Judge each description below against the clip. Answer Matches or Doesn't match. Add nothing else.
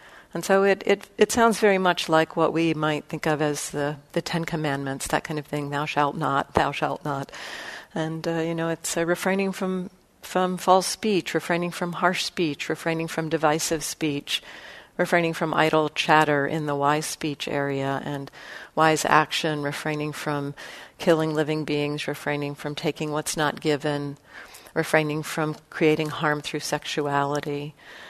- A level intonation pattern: Matches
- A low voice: Doesn't match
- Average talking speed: Matches